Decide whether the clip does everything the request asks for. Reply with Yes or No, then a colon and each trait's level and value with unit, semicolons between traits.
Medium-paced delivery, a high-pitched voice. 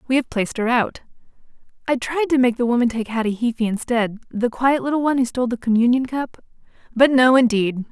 Yes: average, 190 wpm; high, 245 Hz